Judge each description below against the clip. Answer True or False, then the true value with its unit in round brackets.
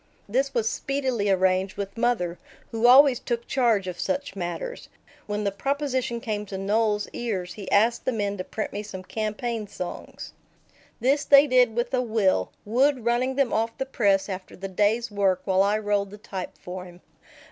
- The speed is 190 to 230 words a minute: False (180 wpm)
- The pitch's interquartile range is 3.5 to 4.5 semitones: True (4.0 semitones)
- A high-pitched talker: True (215 Hz)